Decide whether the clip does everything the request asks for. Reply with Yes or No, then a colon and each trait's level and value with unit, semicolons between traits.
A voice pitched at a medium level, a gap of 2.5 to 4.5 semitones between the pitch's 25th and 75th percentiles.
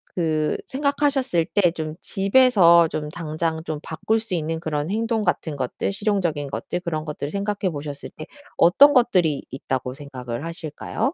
No: medium, 165 Hz; average, 5.1 semitones